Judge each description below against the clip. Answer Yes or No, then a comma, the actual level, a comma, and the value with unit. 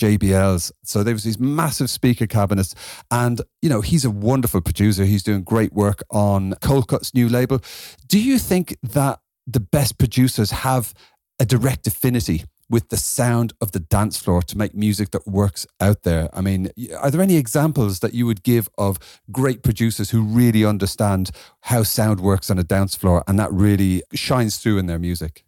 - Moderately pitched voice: No, low, 110 Hz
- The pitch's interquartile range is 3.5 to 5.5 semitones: Yes, average, 4.1 semitones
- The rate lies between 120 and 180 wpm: No, average, 190 wpm